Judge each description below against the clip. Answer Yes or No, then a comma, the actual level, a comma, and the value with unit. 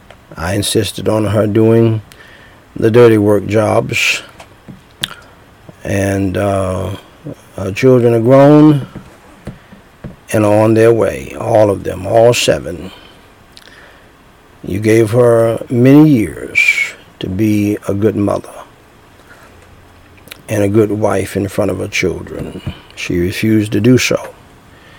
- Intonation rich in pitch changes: No, average, 2.8 semitones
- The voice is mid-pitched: No, low, 110 Hz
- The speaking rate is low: Yes, slow, 120 wpm